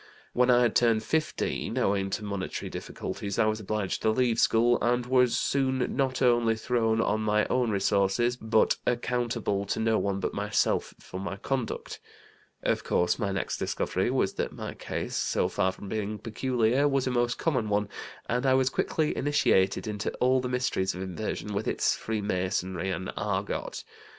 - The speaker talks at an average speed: Yes, average, 175 wpm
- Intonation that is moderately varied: Yes, average, 3.6 semitones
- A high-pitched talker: No, low, 110 Hz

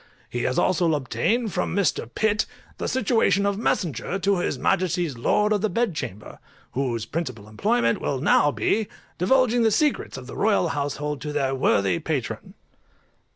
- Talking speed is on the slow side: No, average, 160 wpm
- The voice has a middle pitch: Yes, medium, 165 Hz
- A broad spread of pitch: Yes, wide, 8.1 semitones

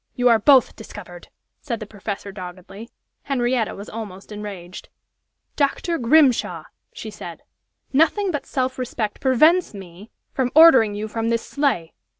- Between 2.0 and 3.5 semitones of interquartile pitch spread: No, average, 4.7 semitones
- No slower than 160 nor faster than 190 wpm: No, average, 140 wpm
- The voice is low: No, high, 230 Hz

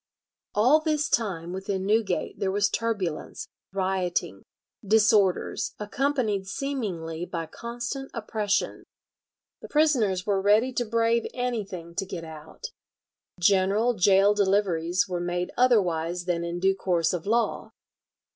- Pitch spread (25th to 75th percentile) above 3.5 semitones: Yes, average, 4.4 semitones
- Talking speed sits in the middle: No, slow, 120 wpm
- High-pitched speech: Yes, high, 200 Hz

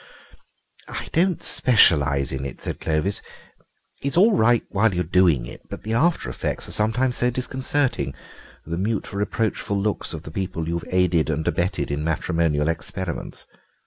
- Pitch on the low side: Yes, very low, 95 Hz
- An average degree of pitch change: No, wide, 6.2 semitones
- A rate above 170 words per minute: No, average, 150 wpm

